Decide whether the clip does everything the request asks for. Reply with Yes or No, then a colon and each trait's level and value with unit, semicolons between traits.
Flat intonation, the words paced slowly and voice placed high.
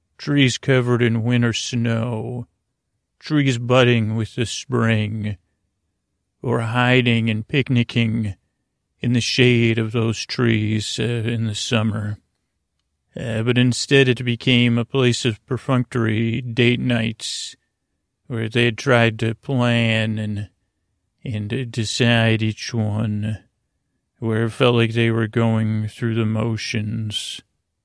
No: narrow, 2.0 semitones; slow, 120 wpm; low, 115 Hz